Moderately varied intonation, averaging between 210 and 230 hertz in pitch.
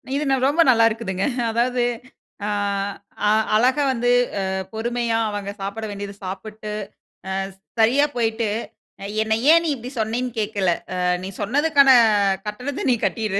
Yes: average, 3.3 semitones; high, 220 Hz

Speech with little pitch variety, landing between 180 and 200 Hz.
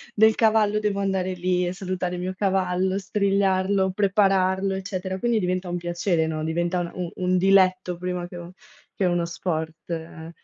Yes: narrow, 1.7 semitones; medium, 185 Hz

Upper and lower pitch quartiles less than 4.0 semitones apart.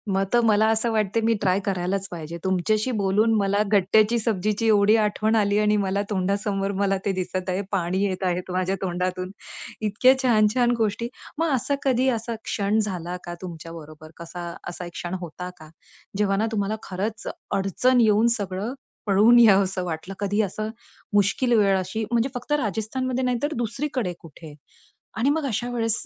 Yes: average, 3.4 semitones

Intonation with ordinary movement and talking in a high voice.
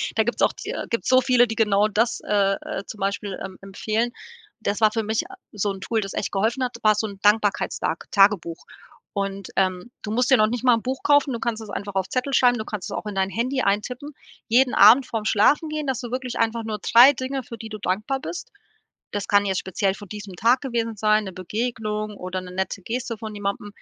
Yes: average, 3.5 semitones; high, 215 Hz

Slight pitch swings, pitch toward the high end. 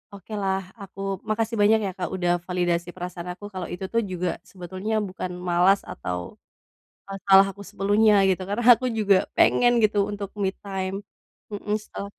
Yes: narrow, 2.2 semitones; high, 195 Hz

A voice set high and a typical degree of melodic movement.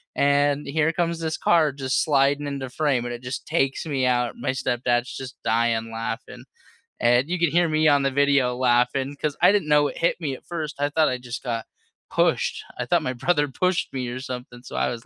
No: low, 135 Hz; average, 3.4 semitones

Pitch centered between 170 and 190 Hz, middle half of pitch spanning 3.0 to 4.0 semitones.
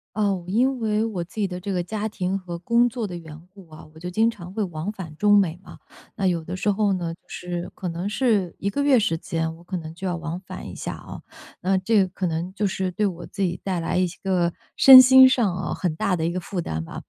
Yes: medium, 185 Hz; average, 3.4 semitones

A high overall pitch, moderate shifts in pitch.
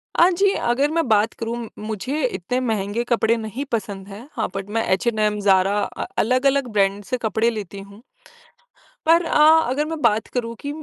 Yes: high, 225 Hz; average, 4.1 semitones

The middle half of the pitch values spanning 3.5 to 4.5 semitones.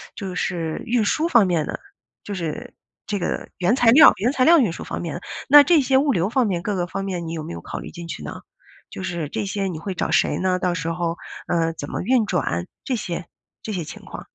No: average, 5.3 semitones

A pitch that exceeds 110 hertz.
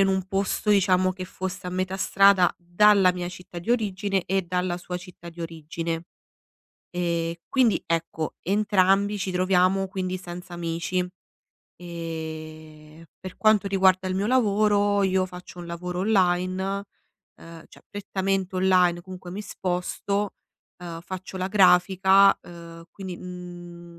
Yes: medium, 185 Hz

